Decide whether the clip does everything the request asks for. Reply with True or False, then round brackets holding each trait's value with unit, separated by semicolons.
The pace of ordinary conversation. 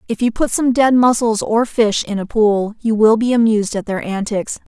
False (225 wpm)